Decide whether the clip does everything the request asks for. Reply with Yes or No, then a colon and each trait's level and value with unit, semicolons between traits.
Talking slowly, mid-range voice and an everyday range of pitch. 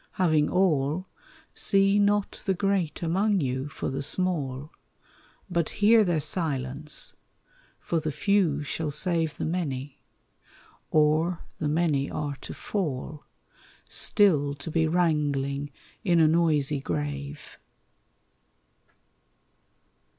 Yes: slow, 105 wpm; medium, 155 Hz; average, 3.9 semitones